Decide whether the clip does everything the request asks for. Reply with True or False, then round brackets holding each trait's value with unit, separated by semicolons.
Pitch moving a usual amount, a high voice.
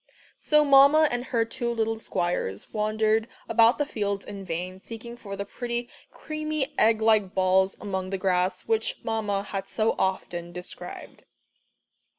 True (3.9 semitones; 220 Hz)